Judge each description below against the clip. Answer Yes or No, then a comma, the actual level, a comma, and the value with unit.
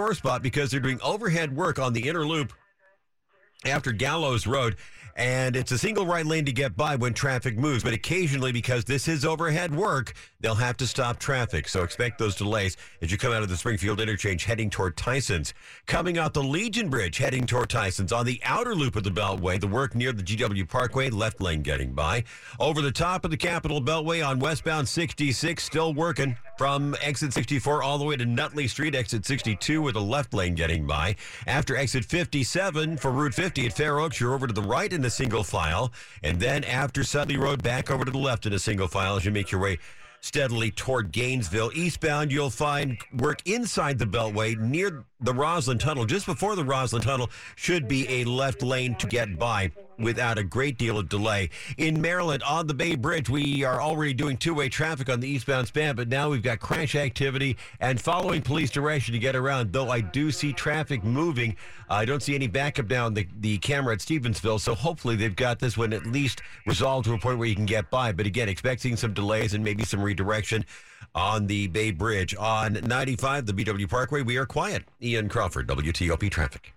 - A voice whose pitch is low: Yes, low, 130 Hz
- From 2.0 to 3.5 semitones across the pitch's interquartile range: No, average, 4.8 semitones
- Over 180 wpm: Yes, fast, 205 wpm